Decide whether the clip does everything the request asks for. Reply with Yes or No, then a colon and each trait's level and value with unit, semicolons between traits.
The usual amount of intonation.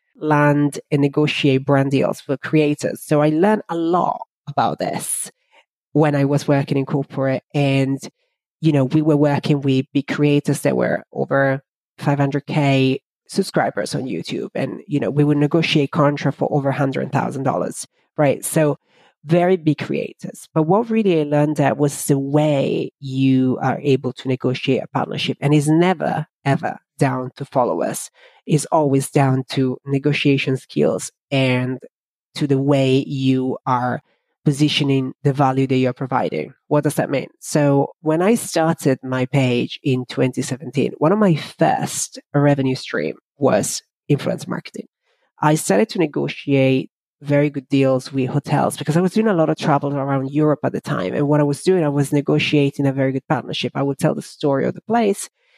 No: narrow, 2.3 semitones